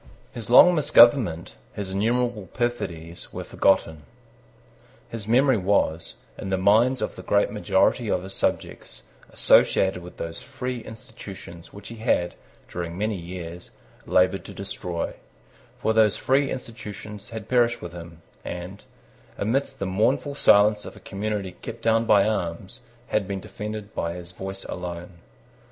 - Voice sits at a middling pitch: No, low, 100 Hz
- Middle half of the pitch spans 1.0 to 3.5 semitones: No, average, 4.1 semitones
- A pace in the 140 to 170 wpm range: Yes, average, 145 wpm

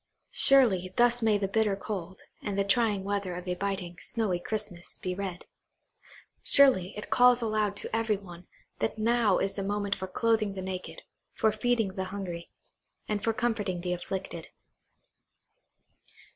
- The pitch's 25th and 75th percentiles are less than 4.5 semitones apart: Yes, average, 2.9 semitones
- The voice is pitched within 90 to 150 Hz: No, high, 200 Hz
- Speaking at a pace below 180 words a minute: Yes, average, 155 wpm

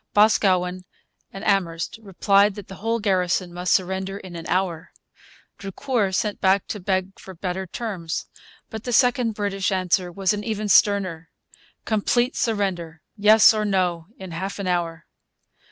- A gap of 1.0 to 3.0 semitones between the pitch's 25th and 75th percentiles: Yes, narrow, 2.6 semitones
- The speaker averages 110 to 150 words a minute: Yes, average, 145 wpm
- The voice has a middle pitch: No, high, 195 Hz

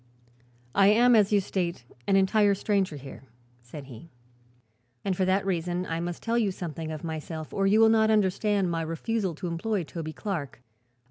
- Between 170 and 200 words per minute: Yes, average, 180 wpm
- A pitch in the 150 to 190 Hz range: Yes, medium, 185 Hz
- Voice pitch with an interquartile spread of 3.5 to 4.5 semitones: Yes, average, 3.9 semitones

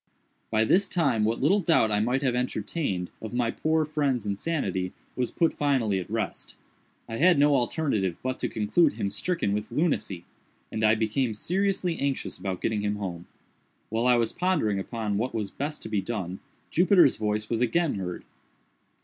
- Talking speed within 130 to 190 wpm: Yes, average, 175 wpm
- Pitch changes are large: Yes, wide, 6.0 semitones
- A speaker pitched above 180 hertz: No, low, 115 Hz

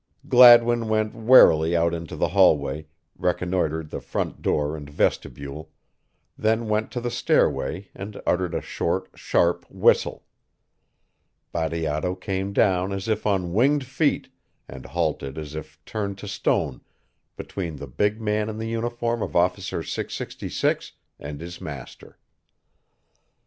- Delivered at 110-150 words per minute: Yes, slow, 135 wpm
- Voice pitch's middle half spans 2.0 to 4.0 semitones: No, average, 5.3 semitones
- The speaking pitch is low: Yes, very low, 95 Hz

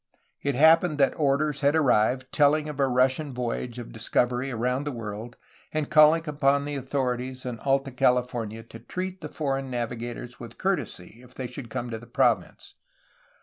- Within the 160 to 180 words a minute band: Yes, average, 175 wpm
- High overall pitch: No, low, 130 Hz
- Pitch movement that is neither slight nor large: Yes, average, 3.2 semitones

